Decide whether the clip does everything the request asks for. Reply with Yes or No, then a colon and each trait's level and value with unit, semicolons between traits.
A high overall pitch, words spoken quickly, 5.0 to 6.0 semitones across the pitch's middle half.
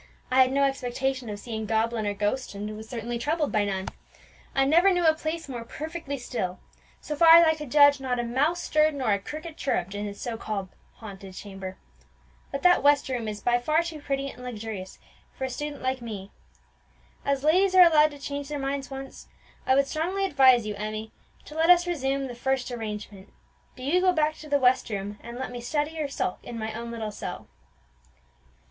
Yes: very high, 260 Hz; fast, 210 wpm; wide, 5.4 semitones